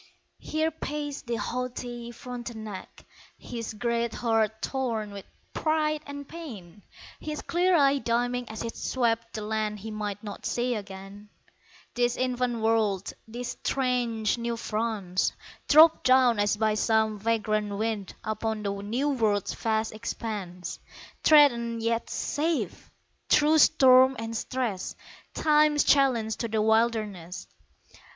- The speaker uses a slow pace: Yes, slow, 125 wpm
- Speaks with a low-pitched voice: No, high, 230 Hz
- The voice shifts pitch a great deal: No, average, 3.1 semitones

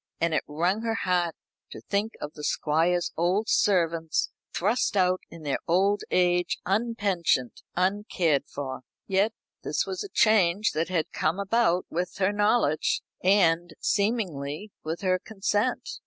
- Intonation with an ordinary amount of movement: Yes, average, 3.8 semitones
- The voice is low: No, medium, 185 Hz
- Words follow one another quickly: No, average, 140 wpm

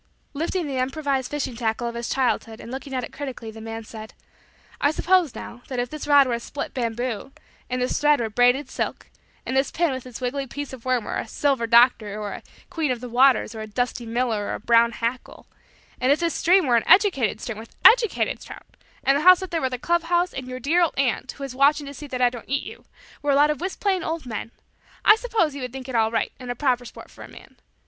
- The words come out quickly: Yes, fast, 255 wpm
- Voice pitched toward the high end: Yes, very high, 260 Hz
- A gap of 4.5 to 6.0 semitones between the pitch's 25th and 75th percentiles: No, average, 3.7 semitones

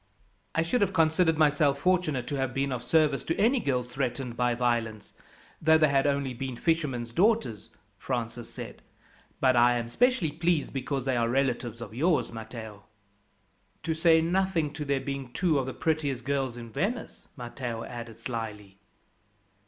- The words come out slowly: No, average, 165 wpm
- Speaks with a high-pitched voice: No, low, 135 Hz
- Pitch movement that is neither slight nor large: Yes, average, 4.9 semitones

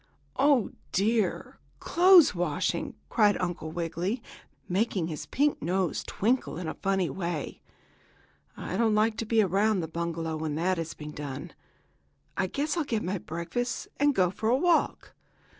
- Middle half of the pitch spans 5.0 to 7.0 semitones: Yes, wide, 5.4 semitones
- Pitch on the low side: No, high, 190 Hz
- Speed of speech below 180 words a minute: Yes, average, 155 wpm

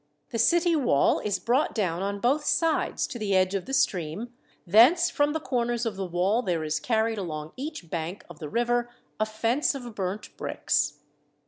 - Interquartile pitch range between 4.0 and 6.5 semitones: Yes, average, 5.1 semitones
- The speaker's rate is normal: Yes, average, 190 wpm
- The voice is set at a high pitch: Yes, high, 220 Hz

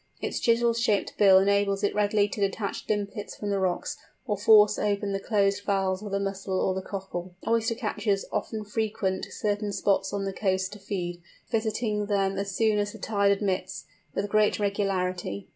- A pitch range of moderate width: No, narrow, 1.5 semitones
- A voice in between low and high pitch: No, high, 200 Hz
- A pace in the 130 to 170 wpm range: No, average, 180 wpm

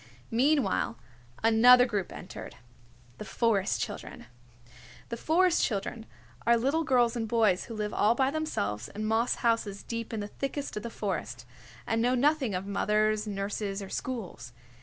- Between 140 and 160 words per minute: Yes, average, 155 wpm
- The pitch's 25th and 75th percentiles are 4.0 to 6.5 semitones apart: No, average, 3.4 semitones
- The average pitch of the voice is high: Yes, high, 225 Hz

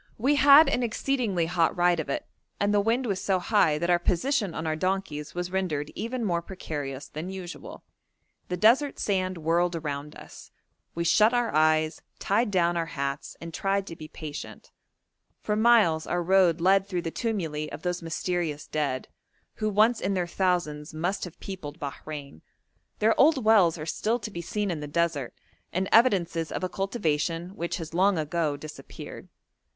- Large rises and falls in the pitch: No, average, 4.3 semitones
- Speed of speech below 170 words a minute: No, average, 175 wpm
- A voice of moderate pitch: Yes, medium, 175 Hz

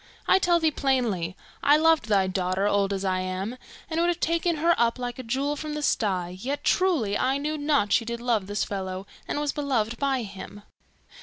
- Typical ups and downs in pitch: No, wide, 6.9 semitones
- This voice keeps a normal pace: No, fast, 215 wpm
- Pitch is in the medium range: No, high, 245 Hz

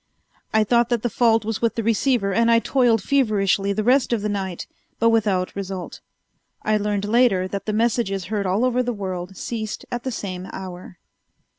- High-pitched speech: Yes, high, 215 Hz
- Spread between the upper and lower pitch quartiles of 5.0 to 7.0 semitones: No, average, 3.2 semitones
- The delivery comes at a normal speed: Yes, average, 190 wpm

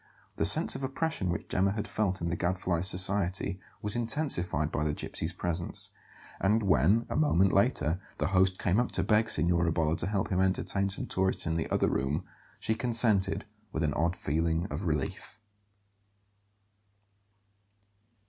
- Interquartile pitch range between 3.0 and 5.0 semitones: Yes, average, 3.7 semitones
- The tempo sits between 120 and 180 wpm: Yes, average, 160 wpm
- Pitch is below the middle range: Yes, very low, 95 Hz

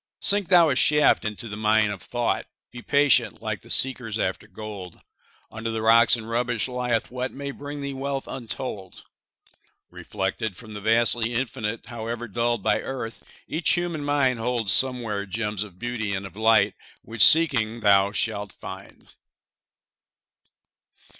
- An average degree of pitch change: Yes, average, 3.4 semitones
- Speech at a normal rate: Yes, average, 150 wpm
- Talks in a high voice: No, low, 115 Hz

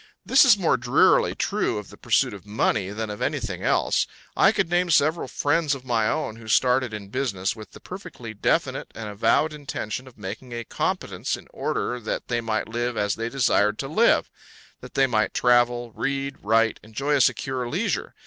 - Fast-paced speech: No, average, 190 wpm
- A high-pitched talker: No, low, 120 Hz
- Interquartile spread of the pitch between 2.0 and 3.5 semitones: No, average, 4.1 semitones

